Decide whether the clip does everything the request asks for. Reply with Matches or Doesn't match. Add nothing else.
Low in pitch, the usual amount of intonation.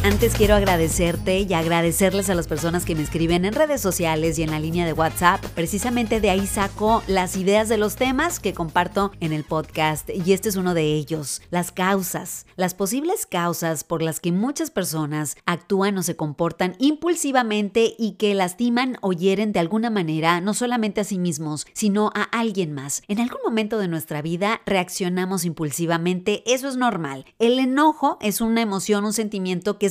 Doesn't match